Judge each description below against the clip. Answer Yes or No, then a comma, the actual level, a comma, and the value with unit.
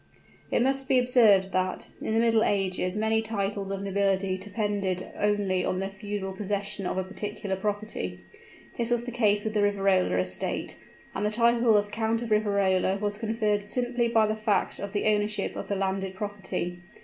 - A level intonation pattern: Yes, narrow, 2.2 semitones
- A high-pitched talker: Yes, high, 205 Hz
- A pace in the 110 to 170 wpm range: No, average, 180 wpm